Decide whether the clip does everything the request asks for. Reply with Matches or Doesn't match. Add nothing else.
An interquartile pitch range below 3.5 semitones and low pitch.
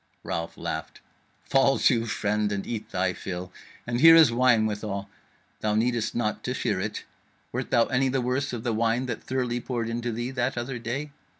Matches